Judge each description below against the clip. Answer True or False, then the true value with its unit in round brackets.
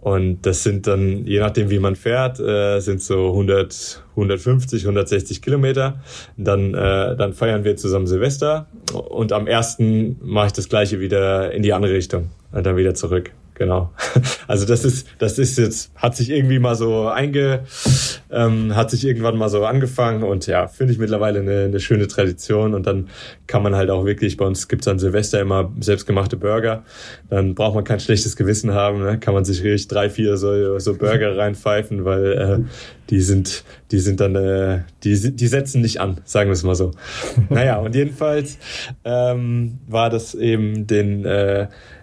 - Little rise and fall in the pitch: False (3.5 semitones)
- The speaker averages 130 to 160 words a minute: False (185 wpm)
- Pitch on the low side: True (105 Hz)